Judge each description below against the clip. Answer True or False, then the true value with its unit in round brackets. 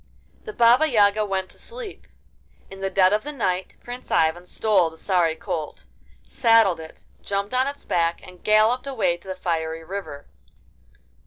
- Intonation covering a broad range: False (5.0 semitones)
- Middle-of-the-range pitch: False (195 Hz)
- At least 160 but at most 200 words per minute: True (165 wpm)